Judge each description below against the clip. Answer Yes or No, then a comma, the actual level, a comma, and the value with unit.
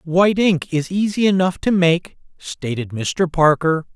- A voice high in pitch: No, medium, 170 Hz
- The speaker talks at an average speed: Yes, average, 150 wpm